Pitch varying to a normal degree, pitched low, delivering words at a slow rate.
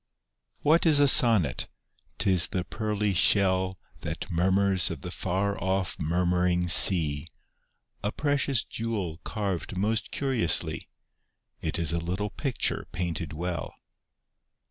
Yes: average, 3.4 semitones; very low, 95 Hz; slow, 125 wpm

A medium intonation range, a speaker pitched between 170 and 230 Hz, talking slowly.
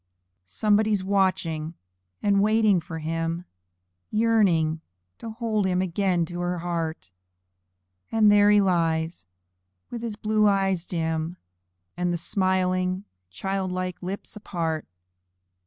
Yes: average, 3.6 semitones; medium, 185 Hz; slow, 115 wpm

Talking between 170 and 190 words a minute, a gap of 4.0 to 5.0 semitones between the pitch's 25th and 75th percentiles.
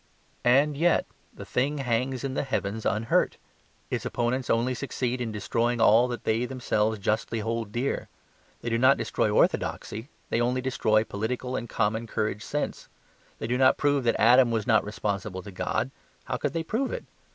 No: average, 175 wpm; average, 2.9 semitones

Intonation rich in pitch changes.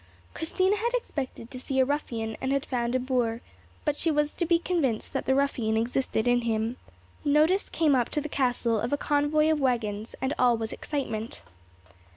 No: average, 4.1 semitones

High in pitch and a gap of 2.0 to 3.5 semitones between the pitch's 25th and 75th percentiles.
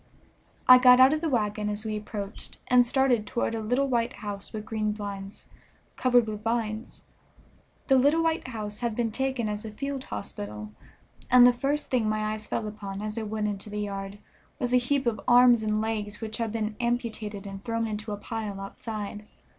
Yes: high, 220 Hz; average, 2.8 semitones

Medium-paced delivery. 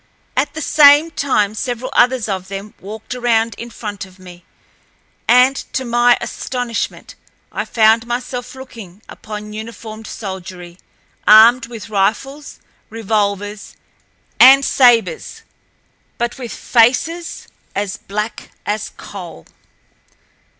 No: slow, 110 wpm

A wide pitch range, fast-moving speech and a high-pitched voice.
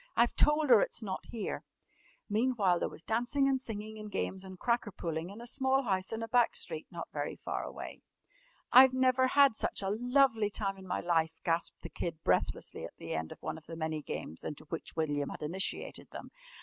Yes: wide, 6.3 semitones; fast, 210 wpm; high, 210 Hz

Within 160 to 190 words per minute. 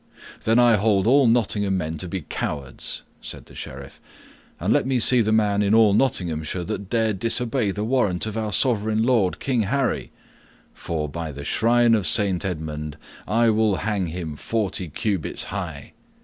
Yes: average, 170 wpm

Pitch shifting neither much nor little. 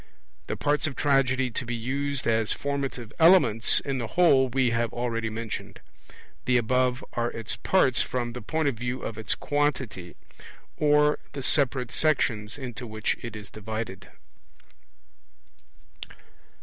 Yes: average, 3.5 semitones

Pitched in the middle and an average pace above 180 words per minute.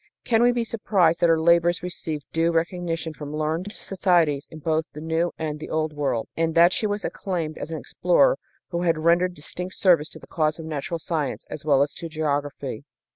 Yes: medium, 165 Hz; fast, 205 wpm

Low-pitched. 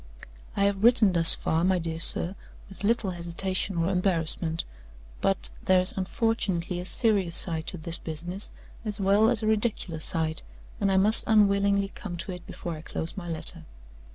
No: medium, 185 Hz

